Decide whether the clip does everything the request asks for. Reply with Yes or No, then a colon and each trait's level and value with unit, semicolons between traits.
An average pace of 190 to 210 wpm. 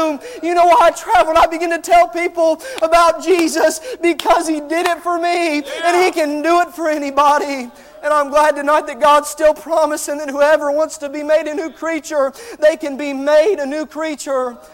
Yes: fast, 205 wpm